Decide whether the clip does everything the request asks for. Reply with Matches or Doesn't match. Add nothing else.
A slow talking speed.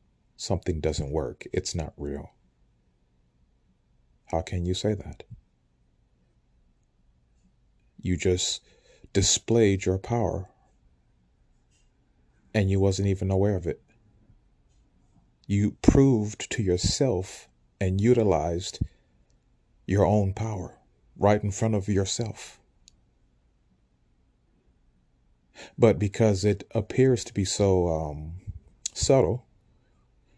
Matches